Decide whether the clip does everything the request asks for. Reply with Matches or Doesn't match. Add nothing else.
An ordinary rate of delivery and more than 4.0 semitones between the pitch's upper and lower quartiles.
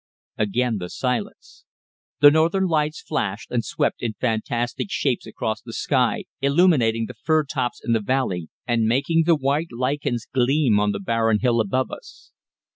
Matches